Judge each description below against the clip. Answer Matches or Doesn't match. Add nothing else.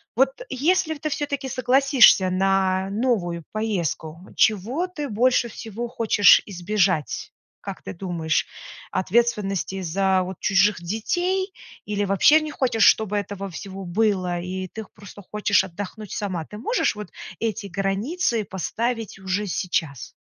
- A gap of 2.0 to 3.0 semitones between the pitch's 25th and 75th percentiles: Doesn't match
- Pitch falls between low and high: Doesn't match